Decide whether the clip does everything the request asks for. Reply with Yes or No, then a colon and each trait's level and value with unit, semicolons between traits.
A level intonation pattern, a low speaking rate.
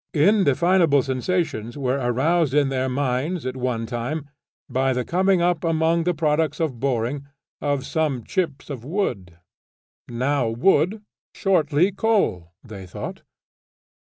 No: average, 4.9 semitones; slow, 130 wpm